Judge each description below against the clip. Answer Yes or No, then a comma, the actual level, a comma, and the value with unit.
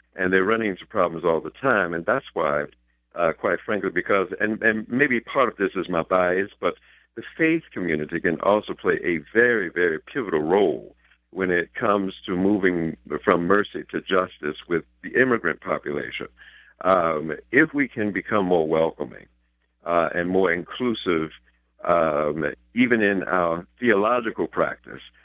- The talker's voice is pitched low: Yes, very low, 90 Hz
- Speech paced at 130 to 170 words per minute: Yes, average, 155 wpm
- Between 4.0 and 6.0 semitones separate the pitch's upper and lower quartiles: Yes, average, 4.6 semitones